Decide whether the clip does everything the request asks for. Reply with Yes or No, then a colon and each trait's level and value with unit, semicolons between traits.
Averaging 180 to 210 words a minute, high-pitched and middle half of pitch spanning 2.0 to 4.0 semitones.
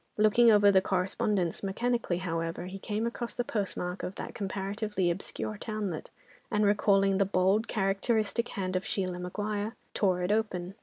No: average, 155 wpm; high, 195 Hz; narrow, 2.6 semitones